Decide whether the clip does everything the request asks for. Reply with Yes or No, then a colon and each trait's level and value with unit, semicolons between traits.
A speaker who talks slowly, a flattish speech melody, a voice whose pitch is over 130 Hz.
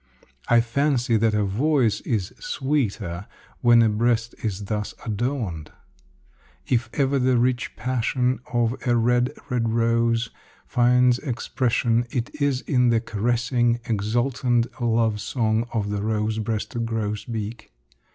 No: slow, 125 wpm; narrow, 2.2 semitones; low, 115 Hz